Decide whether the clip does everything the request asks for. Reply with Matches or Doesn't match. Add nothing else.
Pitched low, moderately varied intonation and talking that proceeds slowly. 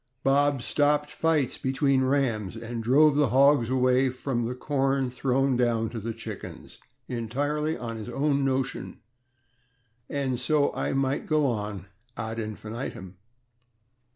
Matches